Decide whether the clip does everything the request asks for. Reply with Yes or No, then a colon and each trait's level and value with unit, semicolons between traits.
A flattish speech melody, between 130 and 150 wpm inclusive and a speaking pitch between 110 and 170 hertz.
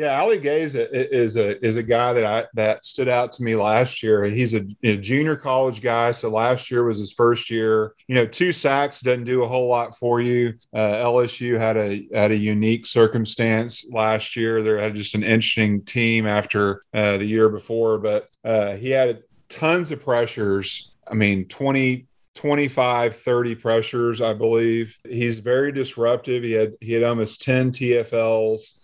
No: narrow, 2.1 semitones; average, 180 wpm; low, 115 Hz